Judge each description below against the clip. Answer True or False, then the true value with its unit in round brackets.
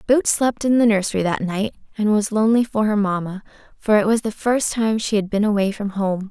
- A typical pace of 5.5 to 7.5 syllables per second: True (5.6 syllables/s)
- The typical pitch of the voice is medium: False (210 Hz)